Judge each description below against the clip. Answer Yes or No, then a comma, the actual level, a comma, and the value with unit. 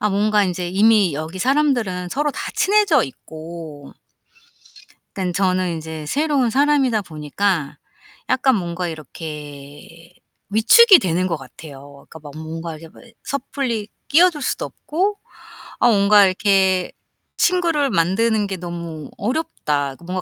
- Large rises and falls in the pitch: Yes, wide, 7.3 semitones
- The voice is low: No, medium, 185 Hz